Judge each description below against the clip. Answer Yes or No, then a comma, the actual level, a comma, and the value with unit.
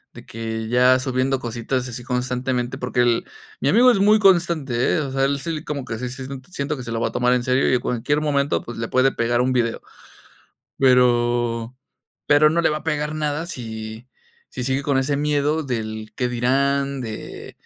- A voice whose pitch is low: Yes, low, 130 Hz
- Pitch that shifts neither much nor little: Yes, average, 3.1 semitones